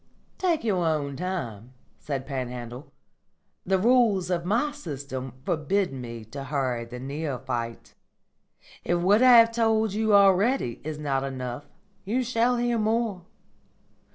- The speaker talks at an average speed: No, slow, 130 wpm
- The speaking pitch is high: No, medium, 170 Hz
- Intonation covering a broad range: Yes, wide, 8.8 semitones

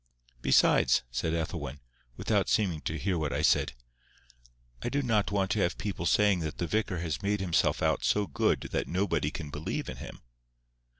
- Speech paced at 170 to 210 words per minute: Yes, average, 180 wpm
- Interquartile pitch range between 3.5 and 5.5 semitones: Yes, average, 4.5 semitones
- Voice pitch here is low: Yes, very low, 90 Hz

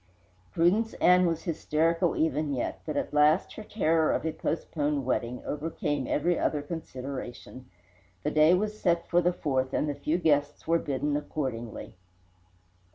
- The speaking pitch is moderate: Yes, medium, 155 Hz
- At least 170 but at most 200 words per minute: No, average, 155 wpm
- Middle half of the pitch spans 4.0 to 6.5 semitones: No, average, 2.8 semitones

